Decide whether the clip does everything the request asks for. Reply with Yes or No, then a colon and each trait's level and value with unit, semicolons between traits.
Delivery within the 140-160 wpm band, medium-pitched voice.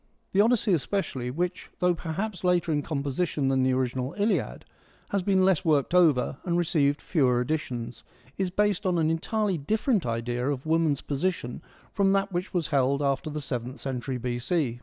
No: average, 170 wpm; medium, 155 Hz